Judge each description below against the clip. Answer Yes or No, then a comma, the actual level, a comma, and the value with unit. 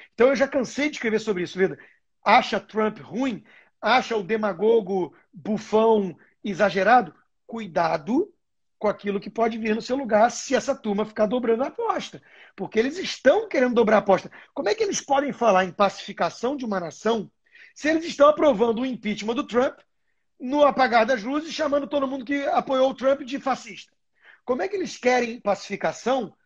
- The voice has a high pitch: Yes, high, 235 Hz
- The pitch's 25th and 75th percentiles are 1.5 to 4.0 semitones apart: No, average, 4.8 semitones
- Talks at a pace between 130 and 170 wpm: No, average, 180 wpm